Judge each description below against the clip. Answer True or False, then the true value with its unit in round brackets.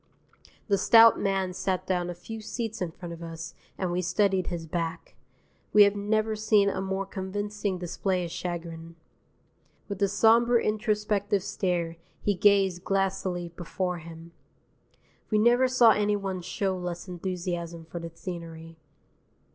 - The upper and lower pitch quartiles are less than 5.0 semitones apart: True (3.0 semitones)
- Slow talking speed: False (145 wpm)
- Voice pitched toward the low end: False (190 Hz)